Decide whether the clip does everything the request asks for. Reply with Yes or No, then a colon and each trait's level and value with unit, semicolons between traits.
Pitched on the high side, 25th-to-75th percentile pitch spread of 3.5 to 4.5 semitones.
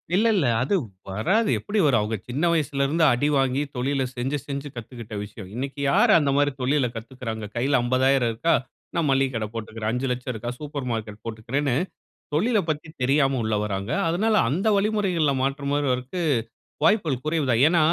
No: low, 135 Hz; average, 4.2 semitones